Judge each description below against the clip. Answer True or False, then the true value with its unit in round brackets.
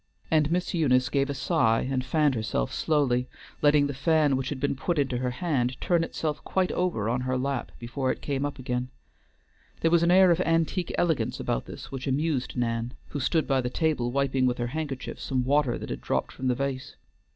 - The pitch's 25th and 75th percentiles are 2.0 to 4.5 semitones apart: True (3.8 semitones)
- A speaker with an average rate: False (210 wpm)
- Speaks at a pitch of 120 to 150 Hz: True (135 Hz)